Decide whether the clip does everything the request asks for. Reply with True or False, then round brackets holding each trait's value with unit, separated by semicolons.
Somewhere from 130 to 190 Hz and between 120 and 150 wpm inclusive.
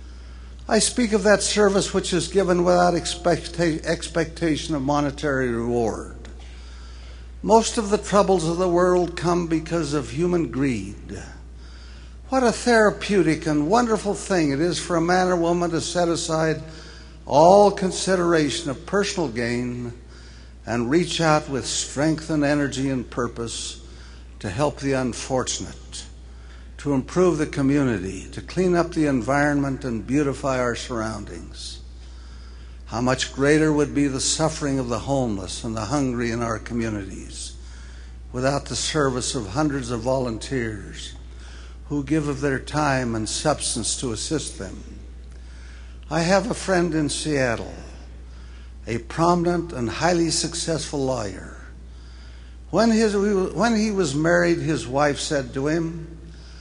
True (140 Hz; 135 wpm)